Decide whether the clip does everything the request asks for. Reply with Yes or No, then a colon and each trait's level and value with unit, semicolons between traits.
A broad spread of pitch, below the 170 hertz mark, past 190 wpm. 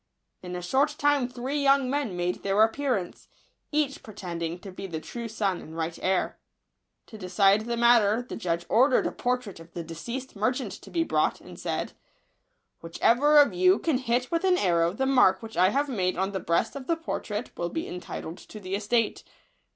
No: wide, 6.3 semitones; high, 220 Hz; fast, 205 wpm